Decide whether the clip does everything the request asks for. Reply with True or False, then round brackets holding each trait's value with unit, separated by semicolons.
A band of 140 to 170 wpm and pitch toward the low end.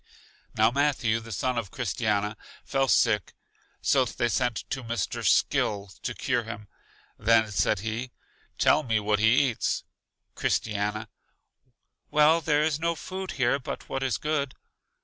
True (145 wpm; 120 Hz)